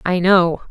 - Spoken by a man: No, female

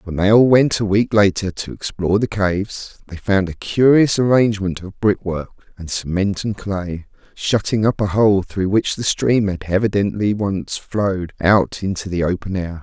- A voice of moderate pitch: No, low, 100 Hz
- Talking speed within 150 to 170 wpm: No, average, 180 wpm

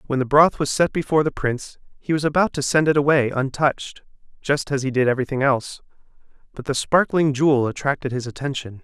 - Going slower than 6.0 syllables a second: No, 6.2 syllables/s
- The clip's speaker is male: Yes, male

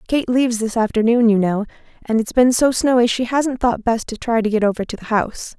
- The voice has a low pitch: No, high, 230 Hz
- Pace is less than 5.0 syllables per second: No, 5.8 syllables/s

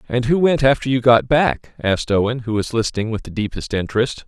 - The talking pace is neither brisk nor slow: No, fast, 225 wpm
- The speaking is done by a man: Yes, male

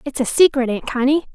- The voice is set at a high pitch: Yes, very high, 265 Hz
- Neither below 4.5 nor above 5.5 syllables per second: No, 5.8 syllables/s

